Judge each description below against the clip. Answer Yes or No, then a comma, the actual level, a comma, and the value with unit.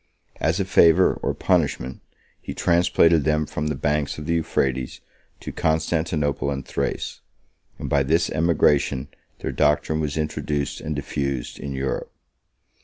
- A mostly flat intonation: Yes, narrow, 2.2 semitones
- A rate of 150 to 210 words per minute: No, average, 140 wpm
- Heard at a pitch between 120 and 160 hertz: No, very low, 75 Hz